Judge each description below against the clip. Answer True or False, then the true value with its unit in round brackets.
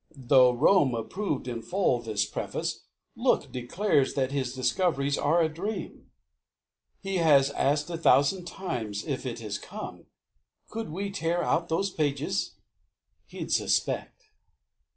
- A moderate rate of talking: False (130 wpm)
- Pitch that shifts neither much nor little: False (5.7 semitones)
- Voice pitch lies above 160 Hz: False (145 Hz)